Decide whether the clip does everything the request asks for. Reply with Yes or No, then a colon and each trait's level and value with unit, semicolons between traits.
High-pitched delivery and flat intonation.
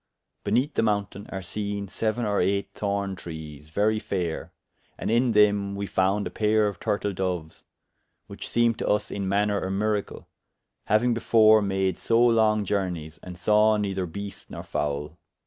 No: low, 100 Hz; narrow, 2.3 semitones